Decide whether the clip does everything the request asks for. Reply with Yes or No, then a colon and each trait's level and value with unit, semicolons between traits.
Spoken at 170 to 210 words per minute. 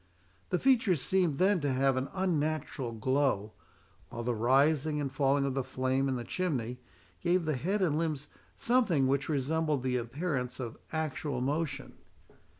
No: average, 155 wpm